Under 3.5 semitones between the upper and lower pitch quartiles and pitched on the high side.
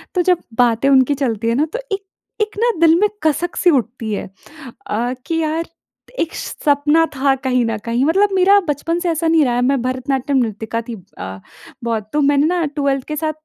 No: average, 5.1 semitones; very high, 280 Hz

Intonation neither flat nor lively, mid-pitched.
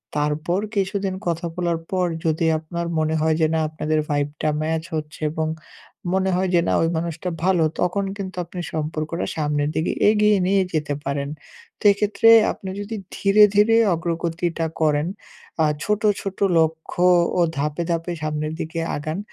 Yes: average, 3.2 semitones; medium, 165 Hz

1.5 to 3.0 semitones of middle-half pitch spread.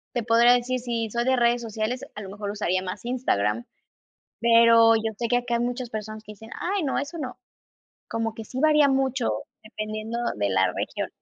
Yes: narrow, 2.4 semitones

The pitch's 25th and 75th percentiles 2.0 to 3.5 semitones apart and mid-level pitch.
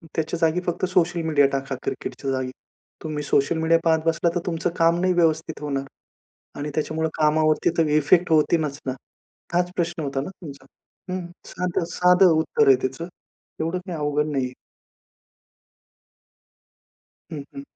Yes: average, 2.8 semitones; medium, 160 Hz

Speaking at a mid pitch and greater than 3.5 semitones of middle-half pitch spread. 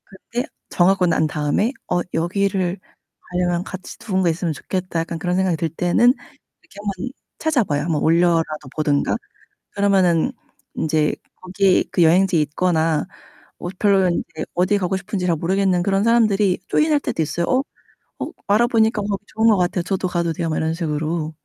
No: medium, 180 Hz; average, 3.2 semitones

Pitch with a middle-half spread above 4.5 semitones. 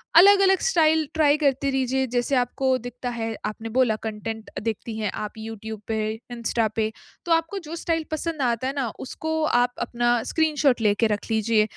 Yes: wide, 5.5 semitones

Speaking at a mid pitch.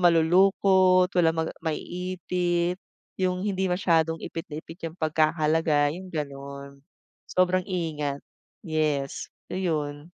Yes: medium, 165 Hz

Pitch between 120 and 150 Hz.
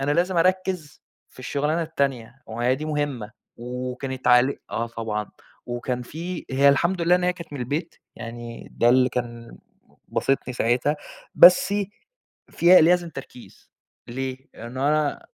Yes: low, 135 Hz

